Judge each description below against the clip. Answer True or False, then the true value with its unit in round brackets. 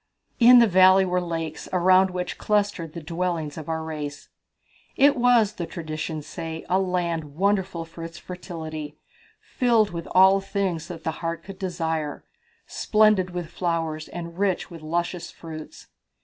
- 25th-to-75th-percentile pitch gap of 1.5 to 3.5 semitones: True (2.9 semitones)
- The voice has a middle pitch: True (175 Hz)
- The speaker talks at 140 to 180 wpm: True (150 wpm)